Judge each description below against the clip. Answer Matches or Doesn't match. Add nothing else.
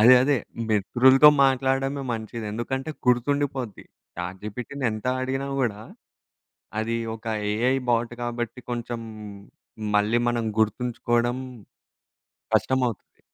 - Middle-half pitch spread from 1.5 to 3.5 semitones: Matches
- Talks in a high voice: Doesn't match